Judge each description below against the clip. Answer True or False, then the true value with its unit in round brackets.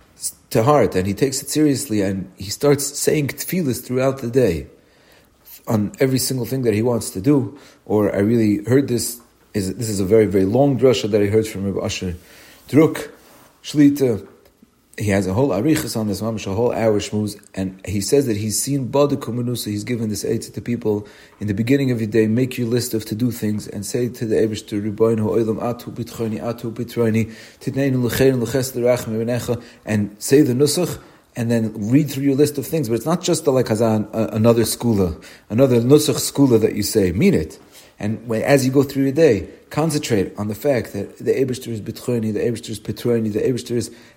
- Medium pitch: False (115 Hz)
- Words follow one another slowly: False (195 wpm)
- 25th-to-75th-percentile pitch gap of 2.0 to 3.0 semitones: False (3.7 semitones)